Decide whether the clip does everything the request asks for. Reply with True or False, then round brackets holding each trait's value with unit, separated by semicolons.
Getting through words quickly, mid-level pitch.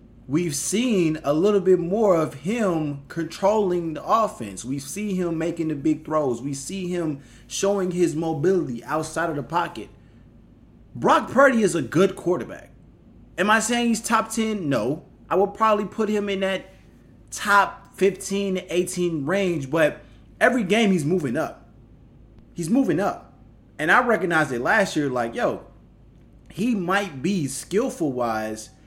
False (155 wpm; 175 Hz)